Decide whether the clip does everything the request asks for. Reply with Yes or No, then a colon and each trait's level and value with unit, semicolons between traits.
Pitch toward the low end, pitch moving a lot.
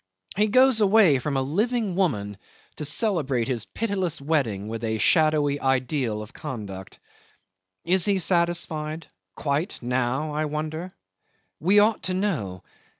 No: medium, 155 Hz; wide, 6.6 semitones